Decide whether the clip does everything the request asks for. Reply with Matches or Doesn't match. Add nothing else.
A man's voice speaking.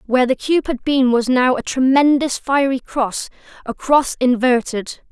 Doesn't match